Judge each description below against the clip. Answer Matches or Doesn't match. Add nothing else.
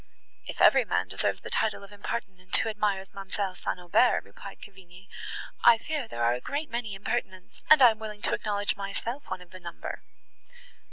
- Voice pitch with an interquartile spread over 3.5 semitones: Doesn't match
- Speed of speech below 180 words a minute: Doesn't match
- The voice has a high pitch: Matches